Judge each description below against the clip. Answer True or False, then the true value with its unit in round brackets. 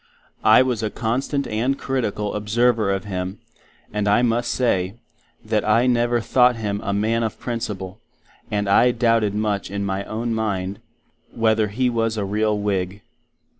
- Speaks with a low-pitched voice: True (110 Hz)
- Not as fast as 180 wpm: True (160 wpm)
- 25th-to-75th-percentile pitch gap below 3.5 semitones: True (2.6 semitones)